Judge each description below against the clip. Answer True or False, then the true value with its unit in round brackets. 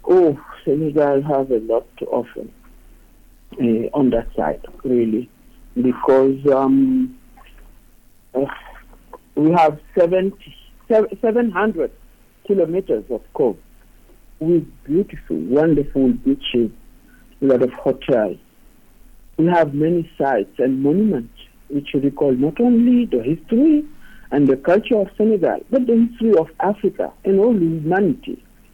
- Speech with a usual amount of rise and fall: False (7.9 semitones)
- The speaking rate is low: True (115 wpm)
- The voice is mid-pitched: True (160 Hz)